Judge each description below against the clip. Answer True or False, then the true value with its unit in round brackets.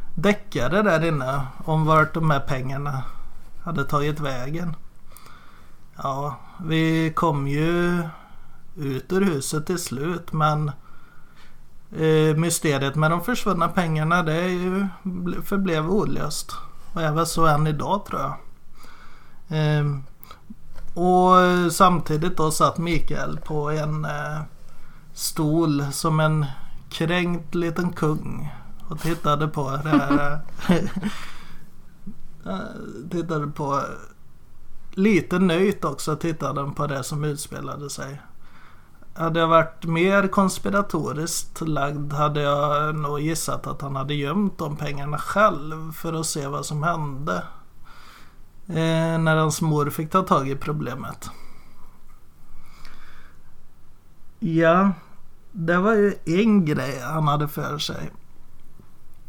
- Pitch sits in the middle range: True (155 Hz)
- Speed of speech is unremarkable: False (115 wpm)